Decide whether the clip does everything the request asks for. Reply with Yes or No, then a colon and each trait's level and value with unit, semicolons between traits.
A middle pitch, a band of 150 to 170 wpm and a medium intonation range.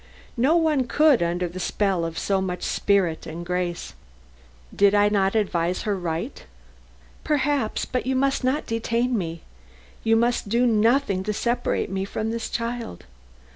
No: high, 215 Hz; average, 155 wpm; average, 5.0 semitones